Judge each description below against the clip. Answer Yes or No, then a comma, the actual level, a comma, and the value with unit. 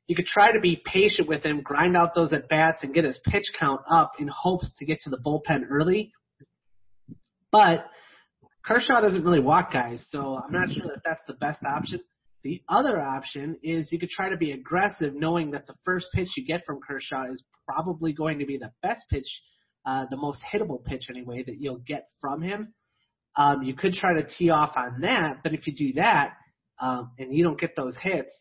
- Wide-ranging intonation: No, average, 4.5 semitones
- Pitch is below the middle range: No, medium, 155 Hz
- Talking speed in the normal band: No, fast, 215 wpm